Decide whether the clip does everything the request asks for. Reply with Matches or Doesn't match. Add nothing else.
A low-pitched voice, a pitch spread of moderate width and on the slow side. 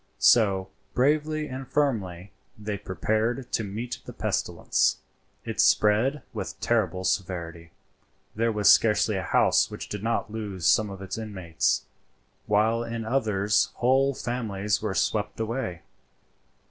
Matches